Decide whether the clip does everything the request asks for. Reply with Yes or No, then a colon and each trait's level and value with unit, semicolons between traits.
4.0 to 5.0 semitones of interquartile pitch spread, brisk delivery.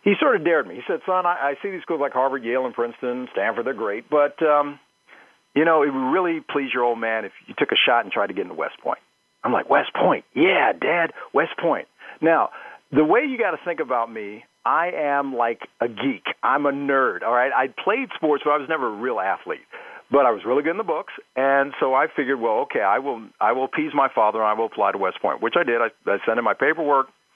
Yes: average, 4.3 semitones; fast, 255 wpm